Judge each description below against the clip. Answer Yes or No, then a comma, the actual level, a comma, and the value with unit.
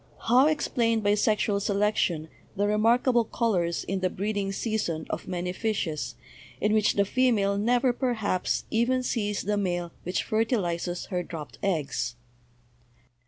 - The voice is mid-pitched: No, high, 205 Hz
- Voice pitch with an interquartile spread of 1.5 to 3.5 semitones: No, average, 4.0 semitones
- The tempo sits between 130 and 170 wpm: Yes, average, 145 wpm